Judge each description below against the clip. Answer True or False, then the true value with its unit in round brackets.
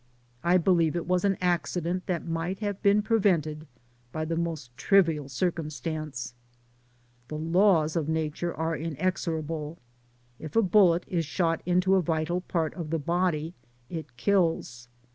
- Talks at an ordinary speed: True (145 wpm)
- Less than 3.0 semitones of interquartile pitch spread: True (2.6 semitones)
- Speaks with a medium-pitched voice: True (165 Hz)